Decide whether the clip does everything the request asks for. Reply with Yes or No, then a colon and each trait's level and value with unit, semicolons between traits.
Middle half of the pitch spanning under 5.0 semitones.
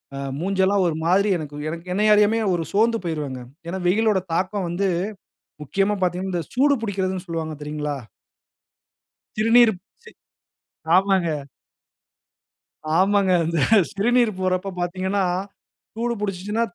Yes: average, 3.2 semitones